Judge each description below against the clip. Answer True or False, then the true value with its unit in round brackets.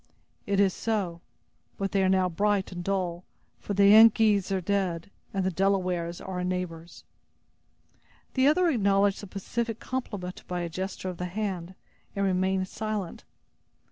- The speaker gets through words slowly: False (155 wpm)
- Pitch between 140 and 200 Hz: True (190 Hz)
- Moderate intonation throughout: False (2.0 semitones)